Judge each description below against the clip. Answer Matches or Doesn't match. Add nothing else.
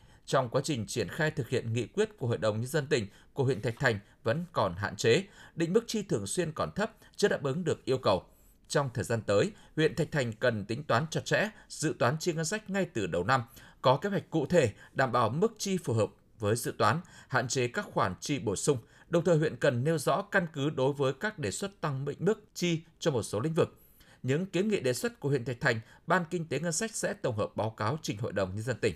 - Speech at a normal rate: Doesn't match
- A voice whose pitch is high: Doesn't match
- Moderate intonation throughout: Doesn't match